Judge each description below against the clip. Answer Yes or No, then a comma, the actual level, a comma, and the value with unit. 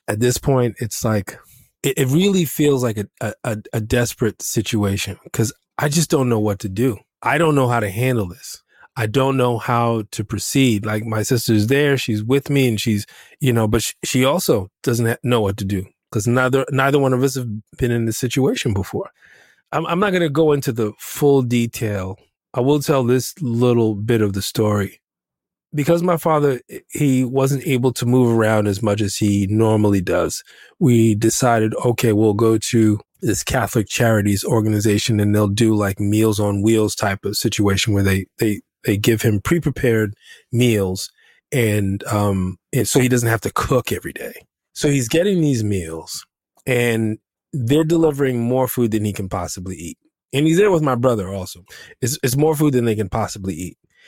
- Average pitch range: Yes, average, 4.0 semitones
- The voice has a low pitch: Yes, low, 115 Hz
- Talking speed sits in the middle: Yes, average, 190 wpm